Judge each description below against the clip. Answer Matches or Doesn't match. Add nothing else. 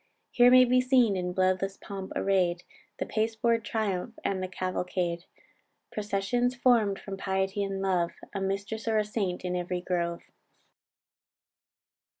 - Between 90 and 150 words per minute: Matches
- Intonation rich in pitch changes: Doesn't match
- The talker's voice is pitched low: Doesn't match